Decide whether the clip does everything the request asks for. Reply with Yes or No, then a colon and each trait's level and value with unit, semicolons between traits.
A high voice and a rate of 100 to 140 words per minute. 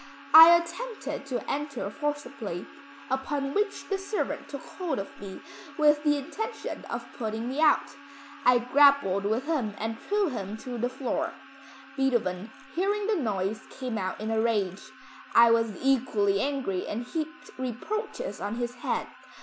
No: very high, 255 Hz; average, 150 wpm